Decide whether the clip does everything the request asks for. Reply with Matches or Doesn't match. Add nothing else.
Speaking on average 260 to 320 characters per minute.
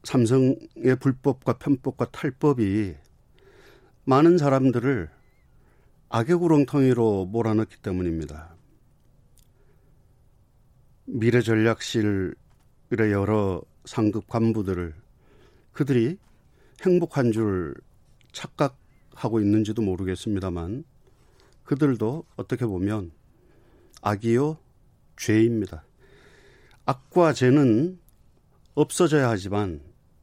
Doesn't match